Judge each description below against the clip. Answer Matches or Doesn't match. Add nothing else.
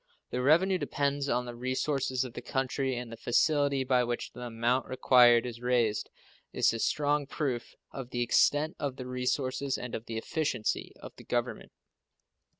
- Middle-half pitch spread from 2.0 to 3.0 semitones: Matches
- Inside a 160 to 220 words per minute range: Matches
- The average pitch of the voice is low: Matches